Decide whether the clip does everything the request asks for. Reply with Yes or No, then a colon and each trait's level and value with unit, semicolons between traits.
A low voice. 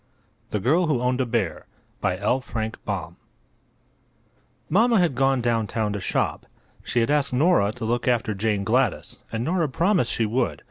Yes: low, 120 Hz